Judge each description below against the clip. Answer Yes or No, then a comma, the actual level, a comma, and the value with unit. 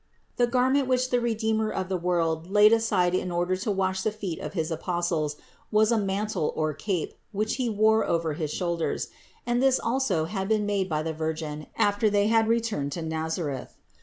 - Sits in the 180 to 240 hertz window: Yes, high, 190 Hz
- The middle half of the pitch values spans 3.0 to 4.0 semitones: No, average, 5.2 semitones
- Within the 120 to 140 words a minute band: No, average, 195 wpm